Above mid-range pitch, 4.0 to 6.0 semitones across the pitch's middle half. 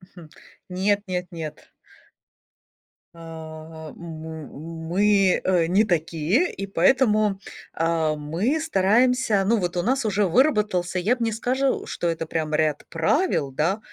No: medium, 180 Hz; average, 4.7 semitones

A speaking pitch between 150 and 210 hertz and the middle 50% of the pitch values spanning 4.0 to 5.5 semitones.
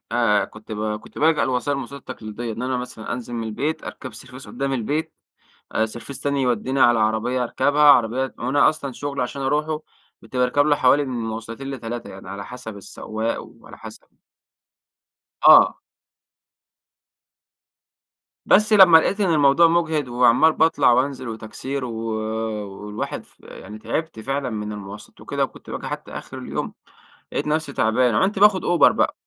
No: low, 130 Hz; average, 4.3 semitones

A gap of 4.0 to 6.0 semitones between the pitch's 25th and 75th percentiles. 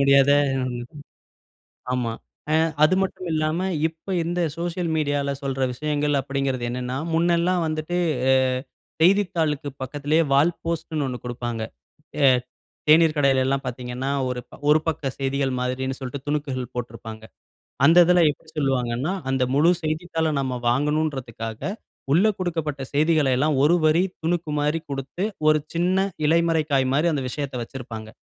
No: average, 3.6 semitones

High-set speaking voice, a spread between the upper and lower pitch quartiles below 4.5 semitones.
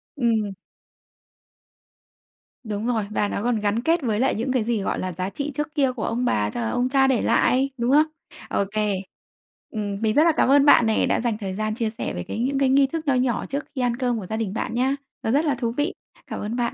Yes: high, 240 Hz; average, 3.8 semitones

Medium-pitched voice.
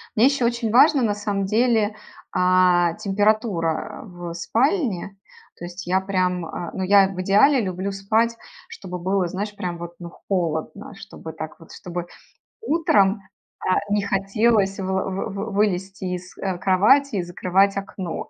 No: high, 195 Hz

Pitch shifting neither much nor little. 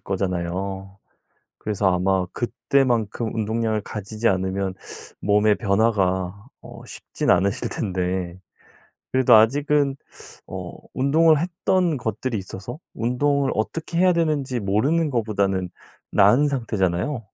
No: wide, 5.9 semitones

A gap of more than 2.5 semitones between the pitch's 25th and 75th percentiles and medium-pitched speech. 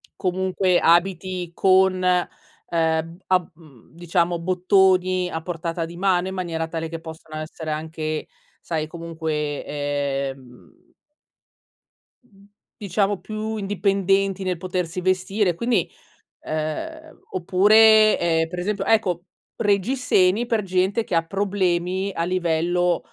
Yes: average, 2.9 semitones; medium, 180 Hz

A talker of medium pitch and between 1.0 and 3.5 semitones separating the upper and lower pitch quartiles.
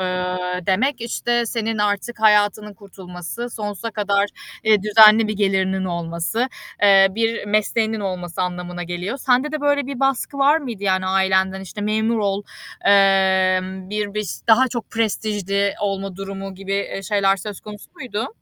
No: high, 205 Hz; average, 2.7 semitones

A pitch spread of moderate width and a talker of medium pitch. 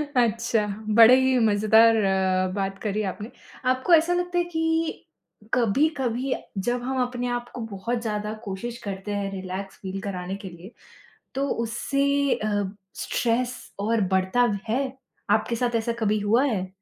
No: average, 3.5 semitones; high, 230 Hz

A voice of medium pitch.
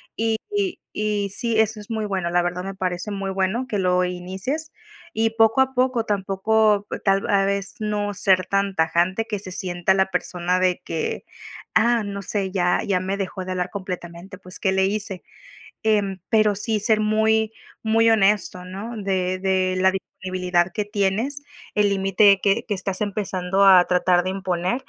No: high, 195 Hz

